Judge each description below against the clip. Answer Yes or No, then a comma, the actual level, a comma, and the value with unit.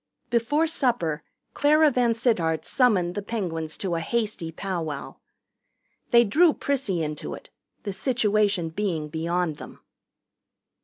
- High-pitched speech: Yes, high, 200 Hz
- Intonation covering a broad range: Yes, wide, 6.6 semitones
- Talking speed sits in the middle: No, slow, 115 wpm